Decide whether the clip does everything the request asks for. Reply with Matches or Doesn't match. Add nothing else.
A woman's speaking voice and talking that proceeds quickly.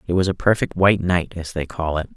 Doesn't match